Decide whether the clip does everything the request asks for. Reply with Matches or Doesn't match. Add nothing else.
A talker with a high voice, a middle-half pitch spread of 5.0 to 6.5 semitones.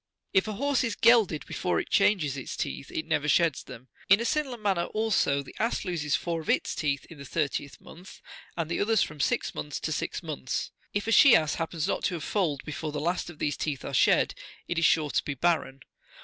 Doesn't match